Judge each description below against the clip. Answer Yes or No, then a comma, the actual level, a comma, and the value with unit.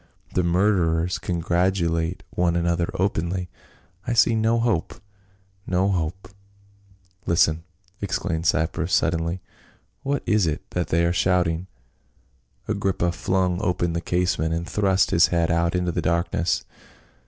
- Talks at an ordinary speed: No, slow, 130 wpm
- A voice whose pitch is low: Yes, very low, 90 Hz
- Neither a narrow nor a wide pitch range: No, narrow, 2.0 semitones